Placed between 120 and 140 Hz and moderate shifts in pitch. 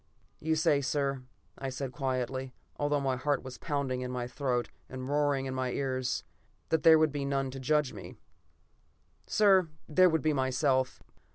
No: low, 135 Hz; narrow, 2.3 semitones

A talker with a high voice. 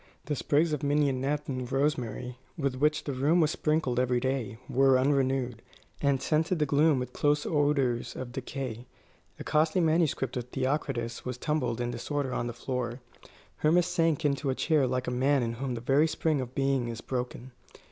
No: low, 135 Hz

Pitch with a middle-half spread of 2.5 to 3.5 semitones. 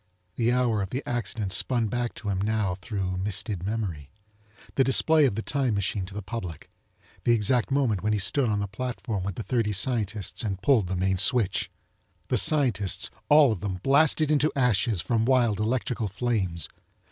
No: average, 4.1 semitones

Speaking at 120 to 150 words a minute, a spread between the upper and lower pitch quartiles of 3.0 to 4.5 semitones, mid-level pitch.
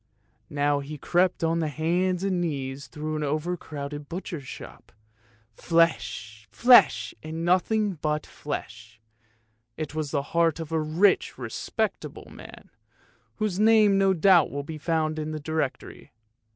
Yes: average, 140 wpm; average, 3.3 semitones; medium, 155 Hz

